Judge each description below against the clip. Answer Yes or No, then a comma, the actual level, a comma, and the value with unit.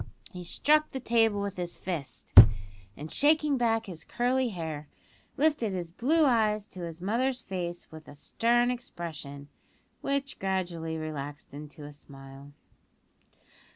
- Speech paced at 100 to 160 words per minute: Yes, slow, 135 wpm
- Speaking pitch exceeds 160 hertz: Yes, medium, 185 Hz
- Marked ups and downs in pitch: Yes, wide, 7.4 semitones